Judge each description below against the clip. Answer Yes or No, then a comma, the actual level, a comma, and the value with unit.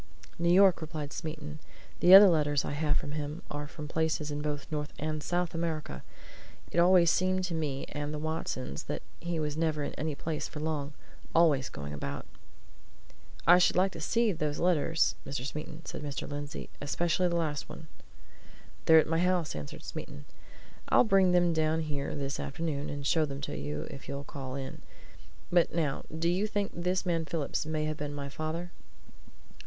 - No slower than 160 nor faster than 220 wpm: Yes, average, 185 wpm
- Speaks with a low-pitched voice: No, medium, 155 Hz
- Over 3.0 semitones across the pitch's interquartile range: No, average, 2.7 semitones